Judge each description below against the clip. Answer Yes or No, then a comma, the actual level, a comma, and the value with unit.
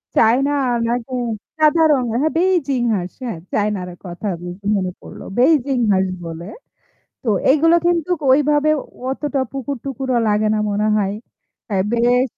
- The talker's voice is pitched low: No, high, 245 Hz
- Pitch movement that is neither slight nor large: No, wide, 5.8 semitones